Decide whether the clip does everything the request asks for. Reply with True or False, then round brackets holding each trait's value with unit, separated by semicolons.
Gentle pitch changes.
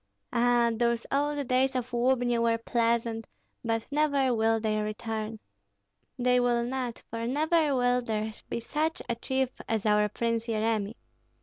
True (2.2 semitones)